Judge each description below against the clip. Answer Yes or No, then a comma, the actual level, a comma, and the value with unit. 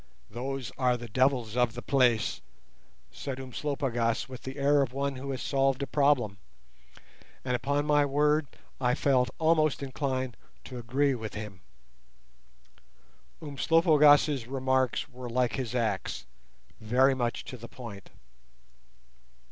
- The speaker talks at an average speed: No, slow, 125 wpm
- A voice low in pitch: Yes, low, 130 Hz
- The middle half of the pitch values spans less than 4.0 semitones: Yes, narrow, 2.6 semitones